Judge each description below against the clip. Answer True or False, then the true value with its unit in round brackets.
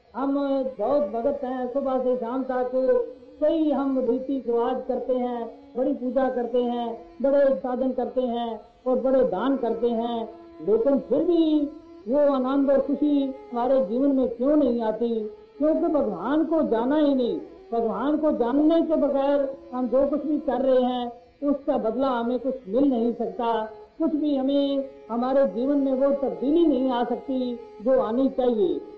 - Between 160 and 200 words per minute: True (165 wpm)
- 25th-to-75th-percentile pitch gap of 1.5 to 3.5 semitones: True (2.7 semitones)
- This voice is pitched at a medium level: False (260 Hz)